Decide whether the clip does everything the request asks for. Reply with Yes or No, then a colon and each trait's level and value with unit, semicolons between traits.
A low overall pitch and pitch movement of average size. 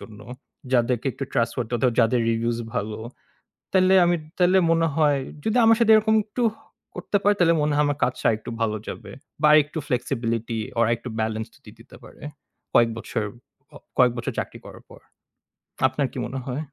No: low, 130 Hz; wide, 6.2 semitones